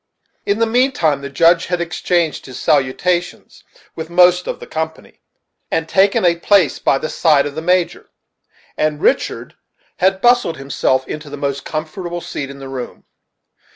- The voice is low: No, medium, 165 Hz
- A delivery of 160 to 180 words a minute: Yes, average, 165 wpm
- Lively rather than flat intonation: No, average, 4.0 semitones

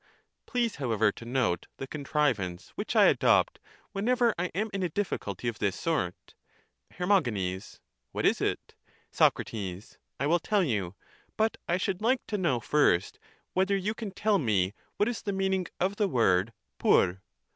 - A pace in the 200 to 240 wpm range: No, average, 165 wpm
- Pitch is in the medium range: Yes, medium, 155 Hz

